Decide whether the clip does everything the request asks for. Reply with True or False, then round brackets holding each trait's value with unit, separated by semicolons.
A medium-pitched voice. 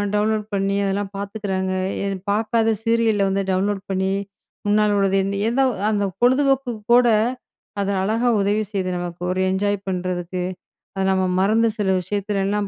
False (200 Hz)